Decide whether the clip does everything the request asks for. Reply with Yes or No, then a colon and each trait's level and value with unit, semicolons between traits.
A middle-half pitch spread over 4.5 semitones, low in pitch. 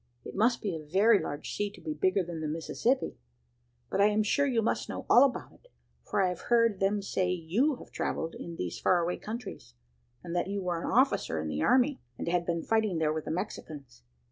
No: average, 5.2 semitones; medium, 185 Hz